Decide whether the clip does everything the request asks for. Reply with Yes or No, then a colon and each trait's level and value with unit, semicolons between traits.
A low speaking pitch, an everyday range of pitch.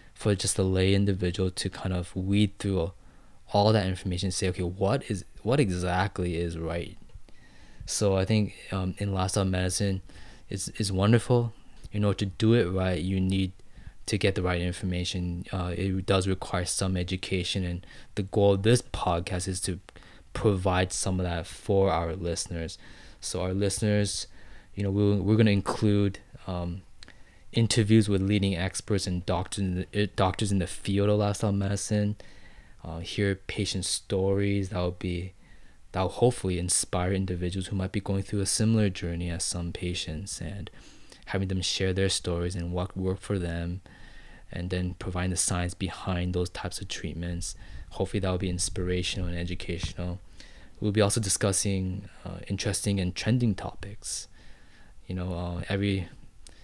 No: very low, 95 Hz; narrow, 2.1 semitones